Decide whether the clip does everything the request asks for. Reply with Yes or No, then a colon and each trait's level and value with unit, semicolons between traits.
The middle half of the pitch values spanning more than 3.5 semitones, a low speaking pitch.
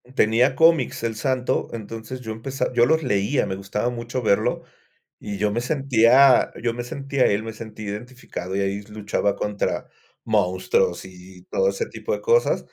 Yes: average, 4.0 semitones; low, 115 Hz